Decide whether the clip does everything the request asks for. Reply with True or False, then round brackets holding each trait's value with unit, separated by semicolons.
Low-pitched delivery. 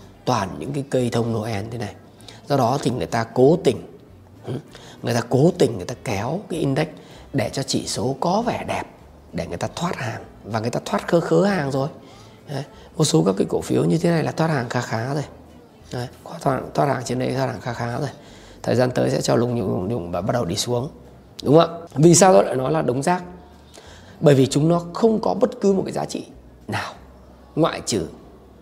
True (125 Hz)